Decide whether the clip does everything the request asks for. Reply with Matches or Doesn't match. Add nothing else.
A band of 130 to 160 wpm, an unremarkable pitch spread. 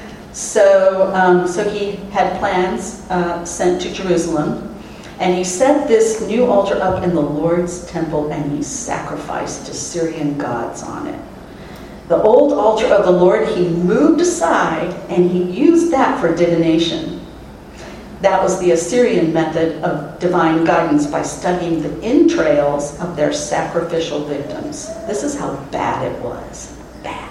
Matches